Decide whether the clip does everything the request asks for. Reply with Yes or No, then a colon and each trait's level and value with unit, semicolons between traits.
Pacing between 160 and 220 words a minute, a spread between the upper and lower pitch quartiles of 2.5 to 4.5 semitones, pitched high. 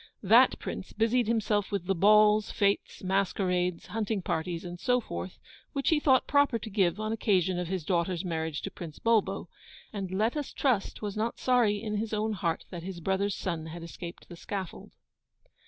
Yes: average, 185 wpm; average, 3.8 semitones; high, 200 Hz